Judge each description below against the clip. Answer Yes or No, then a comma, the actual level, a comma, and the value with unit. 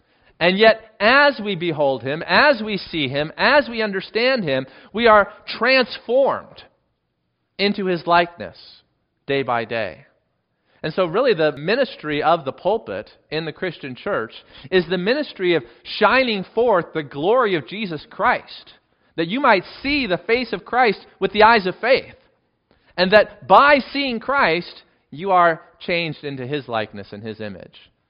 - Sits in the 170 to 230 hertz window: Yes, medium, 185 Hz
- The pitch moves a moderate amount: No, wide, 6.8 semitones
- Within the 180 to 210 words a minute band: No, average, 155 wpm